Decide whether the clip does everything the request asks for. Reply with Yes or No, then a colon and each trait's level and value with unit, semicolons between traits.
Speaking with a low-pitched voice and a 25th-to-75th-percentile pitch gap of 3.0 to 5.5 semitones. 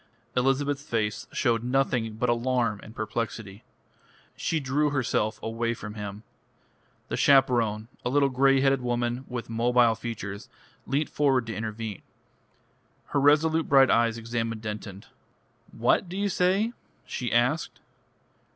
Yes: low, 120 Hz; average, 3.3 semitones